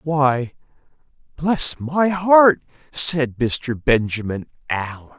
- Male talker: Yes, male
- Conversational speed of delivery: No, slow, 95 wpm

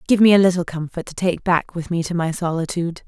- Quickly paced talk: Yes, fast, 255 wpm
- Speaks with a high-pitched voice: No, medium, 175 Hz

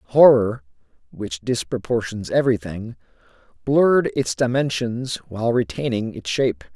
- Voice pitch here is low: Yes, low, 115 Hz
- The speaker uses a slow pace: Yes, slow, 100 wpm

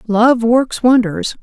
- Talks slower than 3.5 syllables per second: Yes, 3.2 syllables/s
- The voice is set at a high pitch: Yes, high, 230 Hz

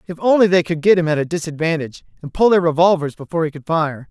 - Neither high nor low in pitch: Yes, medium, 165 Hz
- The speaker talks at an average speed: No, fast, 250 wpm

